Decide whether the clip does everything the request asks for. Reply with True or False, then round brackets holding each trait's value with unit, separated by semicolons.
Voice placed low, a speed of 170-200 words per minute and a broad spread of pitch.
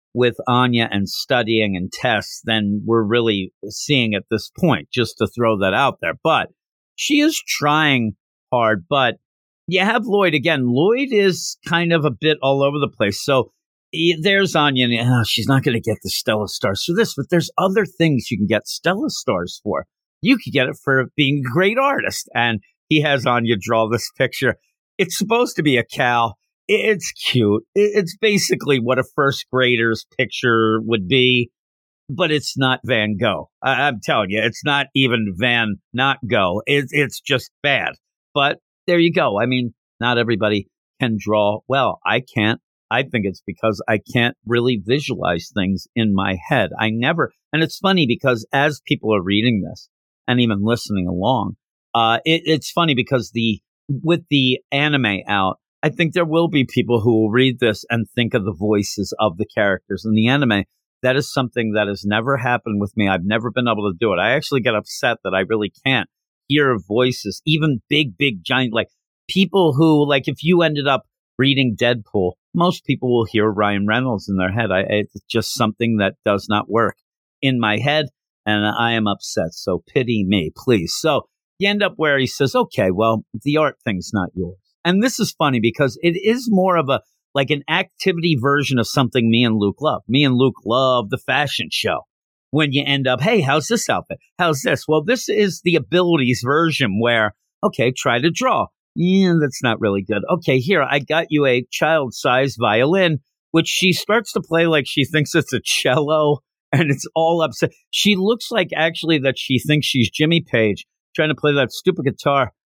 True (130 Hz; 190 wpm; 5.8 semitones)